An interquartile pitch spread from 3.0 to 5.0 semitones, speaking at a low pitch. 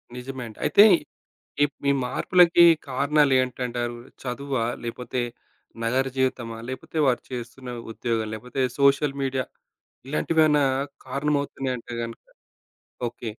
No: narrow, 2.4 semitones; low, 130 Hz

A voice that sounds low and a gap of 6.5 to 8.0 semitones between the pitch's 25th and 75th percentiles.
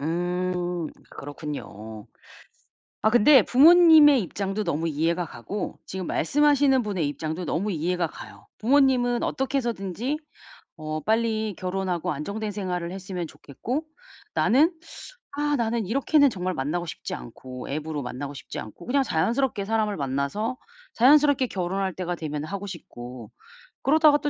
No: high, 190 Hz; wide, 7.6 semitones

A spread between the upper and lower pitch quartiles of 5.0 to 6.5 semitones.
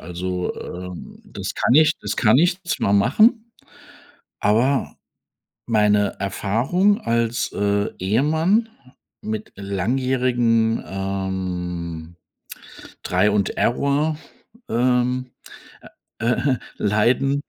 Yes: average, 5.3 semitones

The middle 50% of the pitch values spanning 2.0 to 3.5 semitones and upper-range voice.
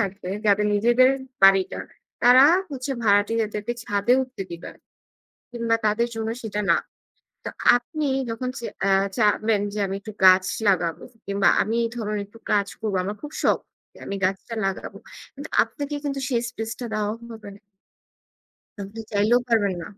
Yes: average, 2.9 semitones; high, 215 Hz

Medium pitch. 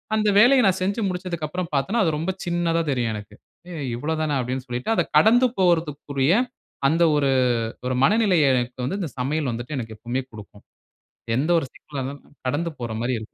Yes: medium, 150 Hz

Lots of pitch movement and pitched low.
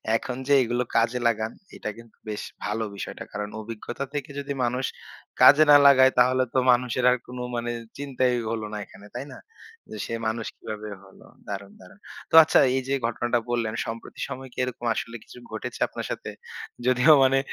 No: narrow, 2.5 semitones; low, 120 Hz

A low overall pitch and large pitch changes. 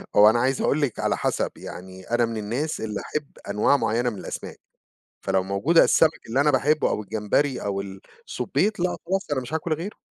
Yes: low, 125 Hz; wide, 6.6 semitones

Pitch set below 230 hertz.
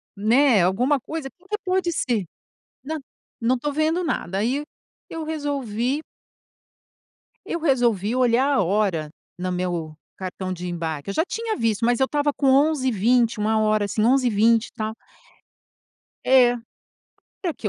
No: high, 240 Hz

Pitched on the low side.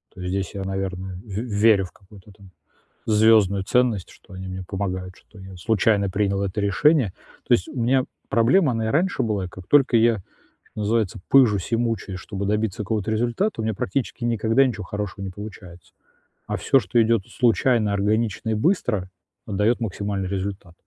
Yes: low, 105 Hz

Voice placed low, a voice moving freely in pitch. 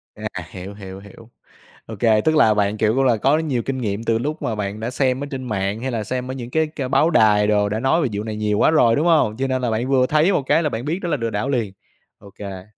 No: low, 120 Hz; average, 4.3 semitones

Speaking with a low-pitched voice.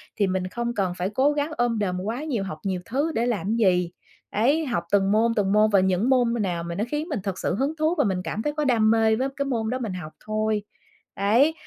No: high, 220 Hz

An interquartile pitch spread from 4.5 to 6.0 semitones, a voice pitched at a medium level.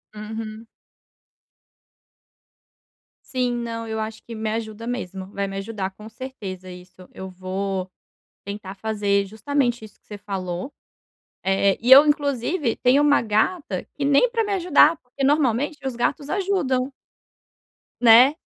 No: wide, 5.4 semitones; high, 225 Hz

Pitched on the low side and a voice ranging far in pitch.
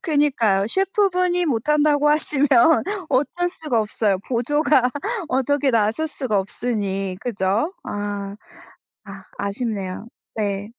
No: high, 245 Hz; wide, 6.6 semitones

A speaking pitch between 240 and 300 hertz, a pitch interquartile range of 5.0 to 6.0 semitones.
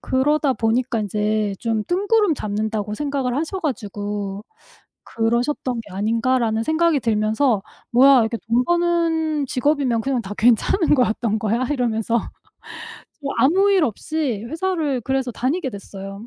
Yes: high, 245 Hz; wide, 5.4 semitones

